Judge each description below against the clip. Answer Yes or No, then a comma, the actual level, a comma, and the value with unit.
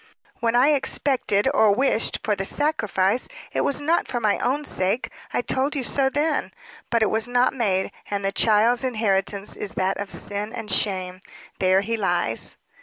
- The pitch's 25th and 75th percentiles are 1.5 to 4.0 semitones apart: No, average, 4.7 semitones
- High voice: Yes, high, 220 Hz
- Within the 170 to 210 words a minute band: Yes, average, 180 wpm